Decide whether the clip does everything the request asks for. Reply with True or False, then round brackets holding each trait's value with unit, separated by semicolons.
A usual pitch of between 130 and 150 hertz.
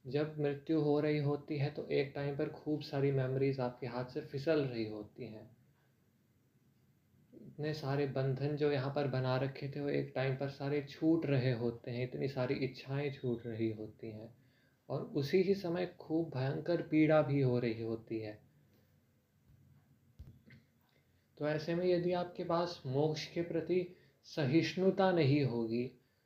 True (140 Hz)